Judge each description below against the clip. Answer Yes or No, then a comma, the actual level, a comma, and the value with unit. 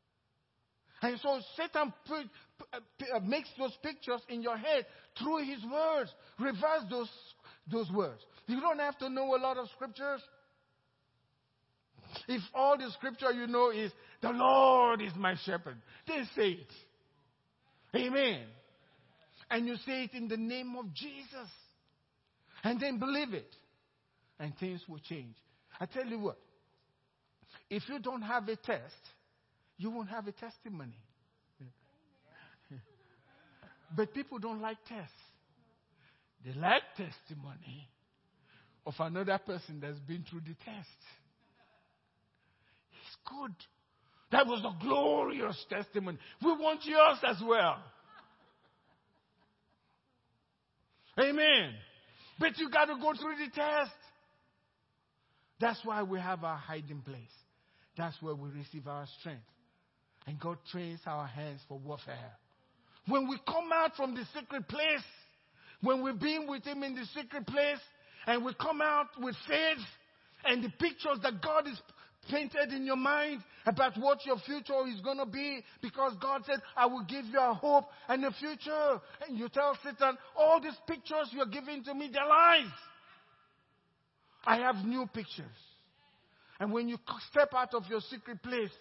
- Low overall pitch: No, high, 240 Hz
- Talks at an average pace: Yes, average, 145 wpm